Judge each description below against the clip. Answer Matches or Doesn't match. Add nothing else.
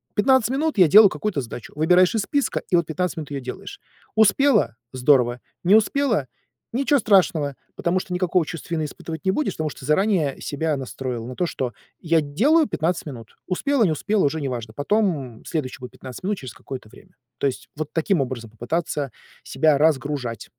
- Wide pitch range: Matches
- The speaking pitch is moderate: Matches